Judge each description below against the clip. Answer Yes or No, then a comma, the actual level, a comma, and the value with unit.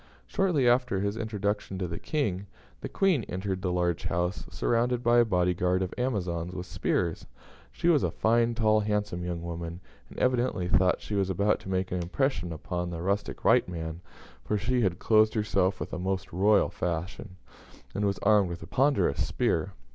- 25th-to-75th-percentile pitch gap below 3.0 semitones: No, average, 3.9 semitones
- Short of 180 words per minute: No, average, 185 wpm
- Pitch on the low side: Yes, very low, 95 Hz